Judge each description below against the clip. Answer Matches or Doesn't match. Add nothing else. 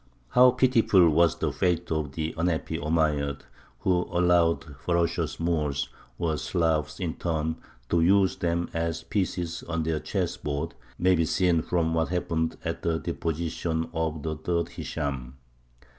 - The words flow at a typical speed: Matches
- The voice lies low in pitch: Matches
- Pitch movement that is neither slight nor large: Doesn't match